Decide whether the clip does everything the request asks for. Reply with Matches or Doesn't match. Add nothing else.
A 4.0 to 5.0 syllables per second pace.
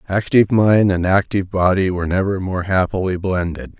Doesn't match